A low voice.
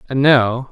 Yes: low, 130 Hz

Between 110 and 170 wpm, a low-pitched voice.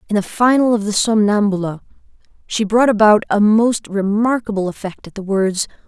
No: average, 165 wpm; high, 210 Hz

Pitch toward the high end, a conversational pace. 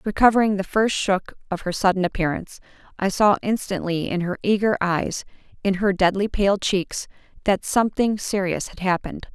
Yes: high, 195 Hz; average, 160 wpm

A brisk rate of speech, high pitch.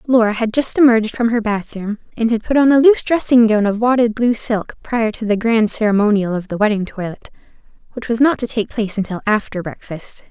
Yes: fast, 220 wpm; high, 225 Hz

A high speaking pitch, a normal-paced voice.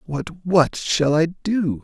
No: medium, 165 Hz; average, 165 wpm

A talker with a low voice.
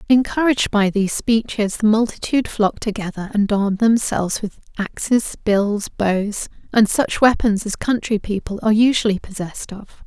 No: high, 215 Hz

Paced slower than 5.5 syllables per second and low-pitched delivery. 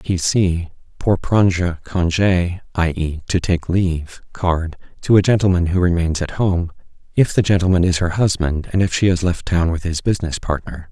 Yes: 4.5 syllables/s; very low, 90 Hz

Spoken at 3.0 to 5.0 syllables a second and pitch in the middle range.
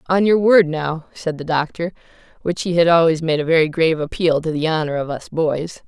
No: 5.5 syllables/s; medium, 165 Hz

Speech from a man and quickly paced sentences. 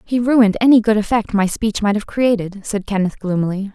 No: female; fast, 210 wpm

